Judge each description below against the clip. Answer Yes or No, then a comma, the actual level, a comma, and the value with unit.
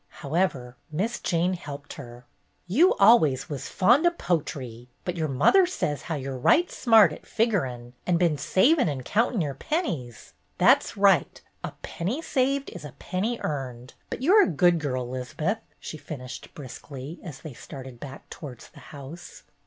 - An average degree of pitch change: No, wide, 7.6 semitones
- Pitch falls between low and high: Yes, medium, 155 Hz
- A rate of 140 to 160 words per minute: No, average, 170 wpm